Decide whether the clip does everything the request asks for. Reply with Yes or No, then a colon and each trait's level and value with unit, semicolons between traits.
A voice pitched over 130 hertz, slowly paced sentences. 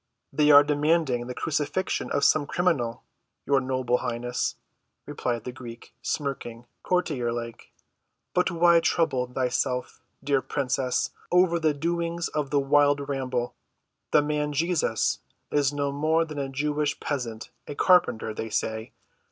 Yes: medium, 140 Hz; slow, 130 wpm